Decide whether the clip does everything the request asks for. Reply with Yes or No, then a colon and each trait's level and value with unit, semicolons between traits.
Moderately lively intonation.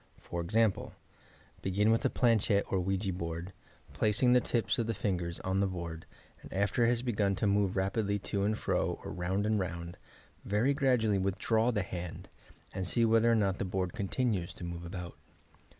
Yes: average, 3.4 semitones